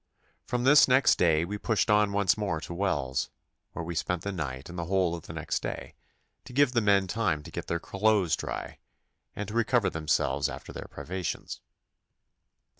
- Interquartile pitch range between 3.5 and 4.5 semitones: Yes, average, 4.1 semitones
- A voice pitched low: Yes, very low, 95 Hz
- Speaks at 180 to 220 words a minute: Yes, average, 190 wpm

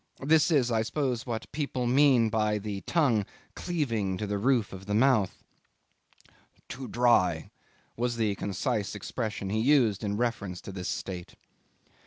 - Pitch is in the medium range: No, low, 110 Hz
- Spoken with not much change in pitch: No, average, 4.1 semitones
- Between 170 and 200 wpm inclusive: No, average, 150 wpm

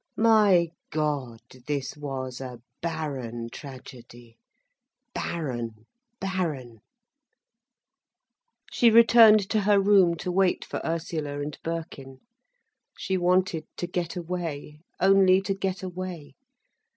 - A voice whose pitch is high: No, medium, 165 Hz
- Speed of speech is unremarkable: No, slow, 105 wpm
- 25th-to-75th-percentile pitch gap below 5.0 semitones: No, wide, 5.5 semitones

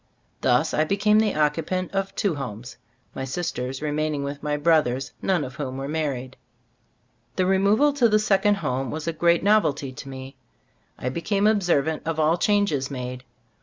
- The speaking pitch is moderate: Yes, medium, 155 Hz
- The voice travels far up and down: Yes, wide, 6.3 semitones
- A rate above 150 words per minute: Yes, average, 170 wpm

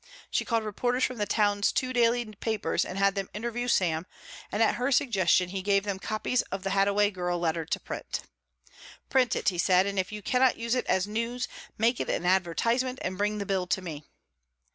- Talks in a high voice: Yes, high, 205 Hz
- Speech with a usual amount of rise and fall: Yes, average, 3.9 semitones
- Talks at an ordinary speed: No, fast, 210 wpm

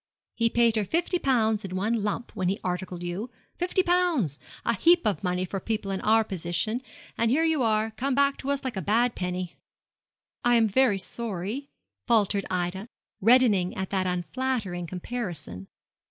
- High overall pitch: Yes, high, 215 Hz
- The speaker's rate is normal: Yes, average, 170 wpm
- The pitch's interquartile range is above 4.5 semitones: Yes, average, 5.0 semitones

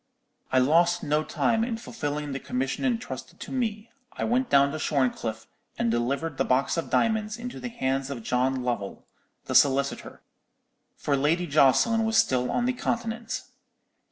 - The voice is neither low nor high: Yes, medium, 150 Hz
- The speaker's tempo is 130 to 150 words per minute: No, average, 160 wpm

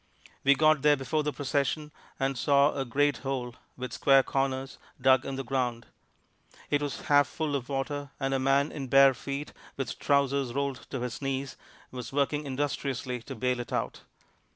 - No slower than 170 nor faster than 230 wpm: Yes, average, 175 wpm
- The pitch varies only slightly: Yes, narrow, 1.5 semitones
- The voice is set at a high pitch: No, low, 135 Hz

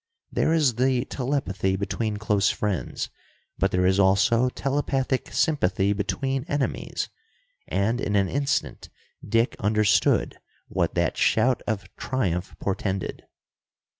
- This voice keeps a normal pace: No, slow, 115 wpm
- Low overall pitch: Yes, low, 110 Hz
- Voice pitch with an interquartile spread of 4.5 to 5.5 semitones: Yes, average, 5.0 semitones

